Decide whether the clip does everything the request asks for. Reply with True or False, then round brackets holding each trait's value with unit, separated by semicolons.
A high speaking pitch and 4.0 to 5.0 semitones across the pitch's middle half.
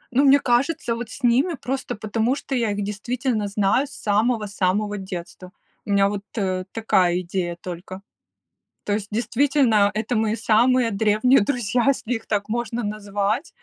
False (215 Hz; 3.3 semitones)